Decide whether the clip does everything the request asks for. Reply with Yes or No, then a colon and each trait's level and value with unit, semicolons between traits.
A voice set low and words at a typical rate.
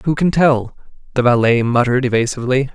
Yes: low, 125 Hz; average, 155 wpm